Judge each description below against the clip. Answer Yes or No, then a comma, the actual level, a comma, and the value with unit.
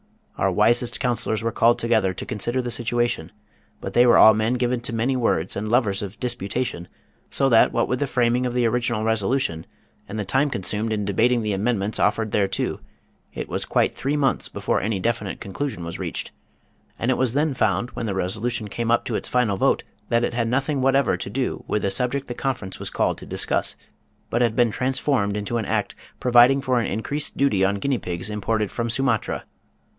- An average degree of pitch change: Yes, average, 3.1 semitones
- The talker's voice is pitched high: No, low, 115 Hz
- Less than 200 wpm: No, fast, 205 wpm